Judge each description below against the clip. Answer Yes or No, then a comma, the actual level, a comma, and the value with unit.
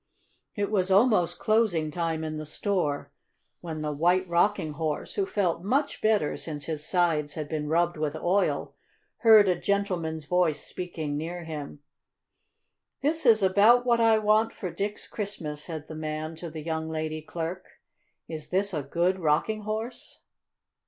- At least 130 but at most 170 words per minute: Yes, average, 160 wpm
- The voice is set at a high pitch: No, medium, 175 Hz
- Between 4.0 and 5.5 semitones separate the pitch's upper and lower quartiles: Yes, average, 4.5 semitones